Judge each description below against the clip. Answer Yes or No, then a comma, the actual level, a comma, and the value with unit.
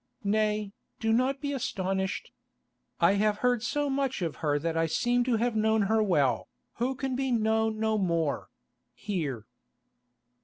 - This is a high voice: Yes, high, 215 Hz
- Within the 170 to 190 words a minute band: No, average, 150 wpm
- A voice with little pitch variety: No, average, 5.3 semitones